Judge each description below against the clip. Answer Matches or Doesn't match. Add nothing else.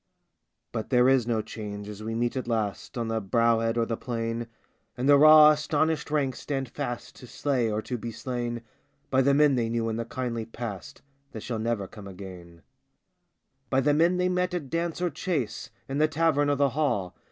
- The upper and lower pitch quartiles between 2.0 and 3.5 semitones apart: Doesn't match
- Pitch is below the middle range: Matches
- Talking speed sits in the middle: Doesn't match